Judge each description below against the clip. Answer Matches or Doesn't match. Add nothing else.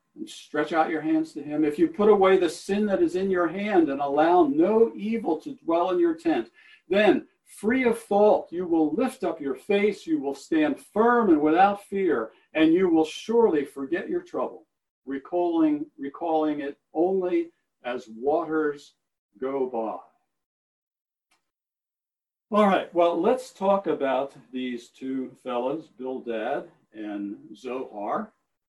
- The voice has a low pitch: Doesn't match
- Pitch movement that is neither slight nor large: Doesn't match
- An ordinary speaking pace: Matches